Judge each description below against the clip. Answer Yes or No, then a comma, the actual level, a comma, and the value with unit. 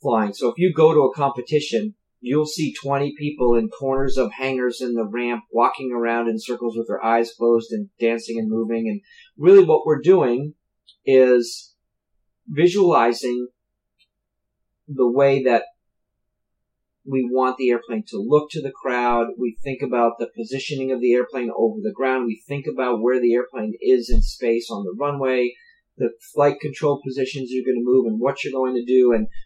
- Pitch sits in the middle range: No, low, 130 Hz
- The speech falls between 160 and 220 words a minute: Yes, average, 180 wpm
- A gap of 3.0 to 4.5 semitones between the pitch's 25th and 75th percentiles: Yes, average, 3.6 semitones